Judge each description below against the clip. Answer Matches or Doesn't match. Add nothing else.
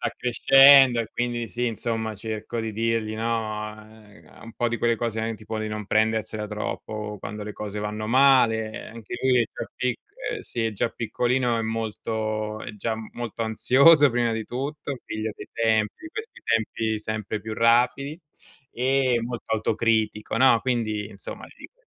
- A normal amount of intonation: Doesn't match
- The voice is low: Matches